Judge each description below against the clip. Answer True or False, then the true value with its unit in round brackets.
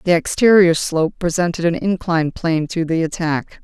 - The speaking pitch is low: False (170 Hz)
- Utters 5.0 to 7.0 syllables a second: True (5.4 syllables/s)